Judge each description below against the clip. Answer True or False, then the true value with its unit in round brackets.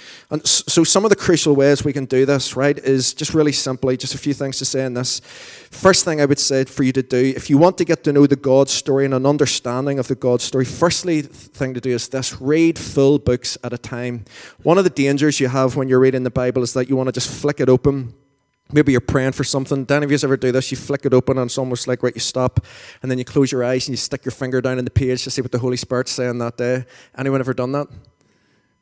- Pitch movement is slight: True (2.0 semitones)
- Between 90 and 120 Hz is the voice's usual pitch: False (135 Hz)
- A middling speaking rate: False (275 wpm)